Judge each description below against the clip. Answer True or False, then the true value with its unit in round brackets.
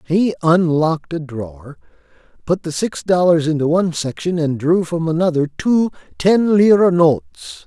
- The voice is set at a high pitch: False (165 Hz)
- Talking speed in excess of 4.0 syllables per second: True (5.0 syllables/s)